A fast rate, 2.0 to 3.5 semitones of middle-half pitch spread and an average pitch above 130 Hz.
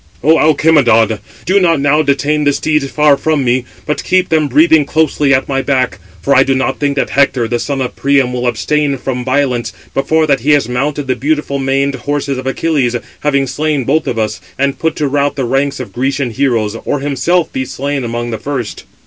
Yes: fast, 210 wpm; narrow, 2.5 semitones; medium, 140 Hz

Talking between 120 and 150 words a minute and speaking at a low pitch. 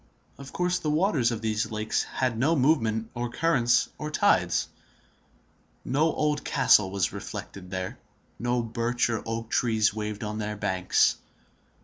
Yes: average, 145 wpm; low, 115 Hz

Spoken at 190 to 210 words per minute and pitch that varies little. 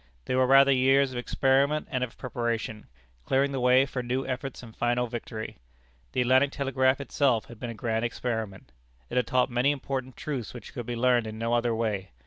Yes: average, 200 wpm; narrow, 2.2 semitones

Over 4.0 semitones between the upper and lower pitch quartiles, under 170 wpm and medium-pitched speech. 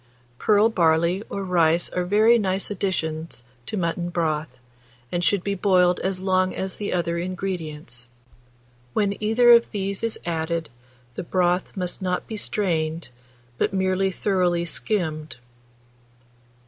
No: average, 2.9 semitones; slow, 135 wpm; medium, 180 Hz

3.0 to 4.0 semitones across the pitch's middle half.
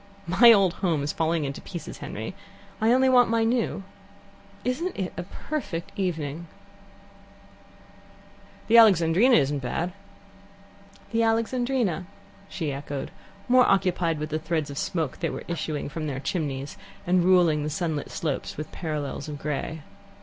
No: average, 5.0 semitones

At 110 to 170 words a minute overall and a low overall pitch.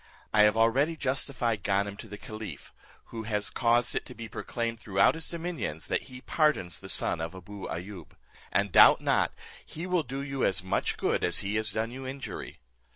No: average, 195 wpm; low, 115 Hz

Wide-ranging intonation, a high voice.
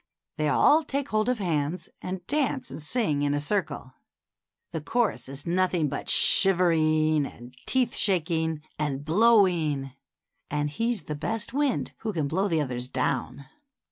No: wide, 6.4 semitones; medium, 160 Hz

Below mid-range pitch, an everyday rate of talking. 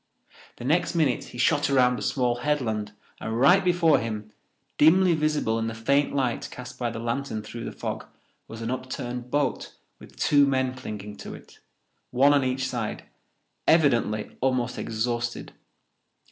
Yes: low, 125 Hz; average, 160 wpm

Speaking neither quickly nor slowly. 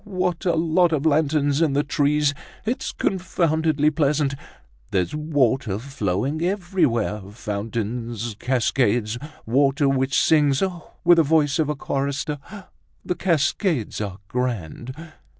No: slow, 120 wpm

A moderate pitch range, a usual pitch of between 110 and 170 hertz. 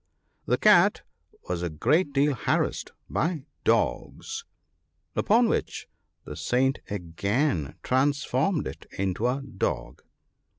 No: wide, 7.2 semitones; low, 135 Hz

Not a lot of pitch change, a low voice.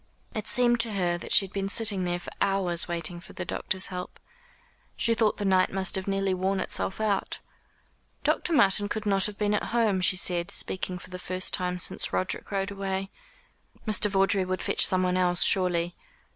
No: narrow, 1.9 semitones; high, 190 Hz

